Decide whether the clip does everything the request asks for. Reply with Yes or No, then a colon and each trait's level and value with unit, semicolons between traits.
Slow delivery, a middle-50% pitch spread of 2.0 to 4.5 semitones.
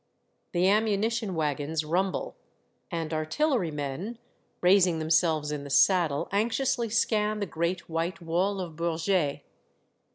Yes: slow, 125 wpm; average, 4.2 semitones